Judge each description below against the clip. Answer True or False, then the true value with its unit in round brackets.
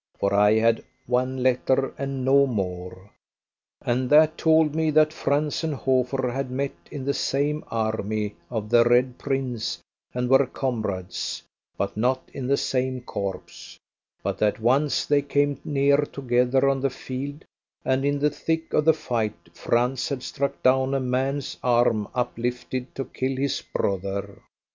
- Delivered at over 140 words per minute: True (155 wpm)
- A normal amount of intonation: True (3.1 semitones)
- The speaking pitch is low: True (130 Hz)